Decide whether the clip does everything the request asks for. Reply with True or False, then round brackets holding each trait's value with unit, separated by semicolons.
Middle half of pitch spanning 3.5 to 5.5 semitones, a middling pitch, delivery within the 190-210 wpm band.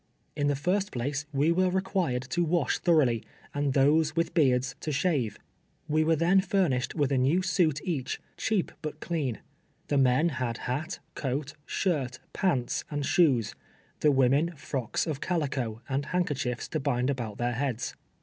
False (4.5 semitones; 145 Hz; 165 wpm)